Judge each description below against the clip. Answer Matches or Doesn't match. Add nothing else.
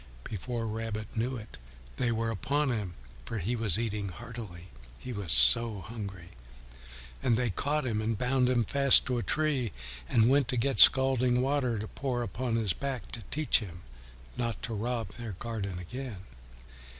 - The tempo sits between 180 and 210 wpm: Doesn't match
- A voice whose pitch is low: Matches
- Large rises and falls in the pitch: Doesn't match